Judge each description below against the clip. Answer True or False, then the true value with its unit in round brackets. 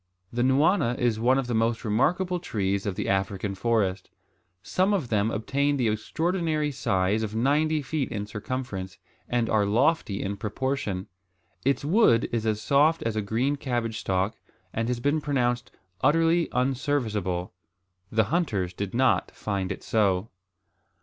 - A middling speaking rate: True (150 wpm)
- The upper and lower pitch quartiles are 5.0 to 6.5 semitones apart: True (5.4 semitones)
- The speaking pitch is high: False (115 Hz)